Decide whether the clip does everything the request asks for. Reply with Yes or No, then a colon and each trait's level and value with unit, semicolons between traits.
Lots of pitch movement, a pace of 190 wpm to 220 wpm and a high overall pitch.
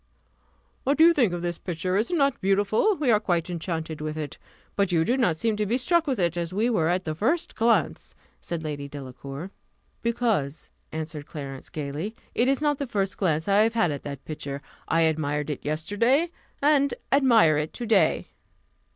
No: wide, 7.1 semitones; average, 195 wpm; medium, 180 Hz